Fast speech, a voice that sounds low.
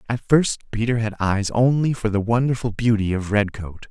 No: average, 185 wpm; low, 110 Hz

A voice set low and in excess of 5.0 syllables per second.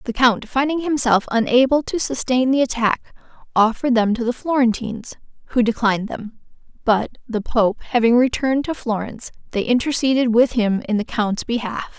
No: high, 240 Hz; 5.4 syllables/s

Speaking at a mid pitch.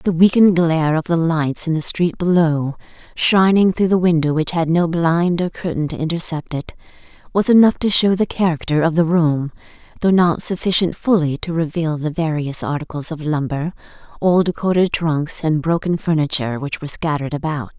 Yes: medium, 165 Hz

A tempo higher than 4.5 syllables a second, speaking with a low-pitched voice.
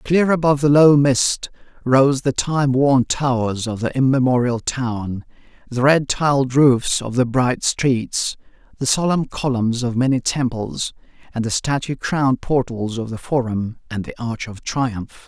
No: 4.2 syllables/s; low, 130 Hz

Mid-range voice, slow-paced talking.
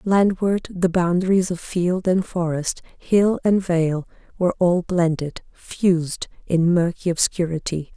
Yes: medium, 175 Hz; slow, 130 wpm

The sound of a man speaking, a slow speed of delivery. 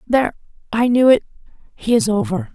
No: female; slow, 120 wpm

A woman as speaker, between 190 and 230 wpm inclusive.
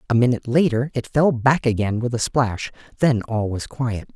No: male; average, 200 wpm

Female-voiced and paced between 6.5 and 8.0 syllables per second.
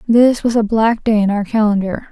No: female; 5.2 syllables/s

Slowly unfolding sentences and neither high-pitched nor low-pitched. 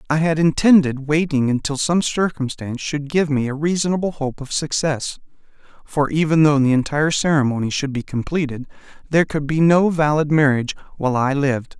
No: average, 170 wpm; medium, 150 Hz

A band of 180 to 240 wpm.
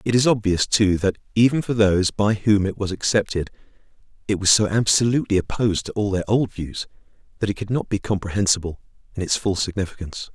Yes: average, 190 wpm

